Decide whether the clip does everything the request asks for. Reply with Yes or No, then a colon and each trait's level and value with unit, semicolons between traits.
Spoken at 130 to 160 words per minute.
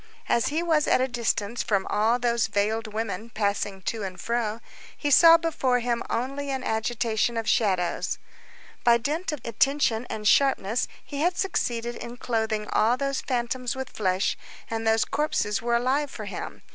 No: average, 170 wpm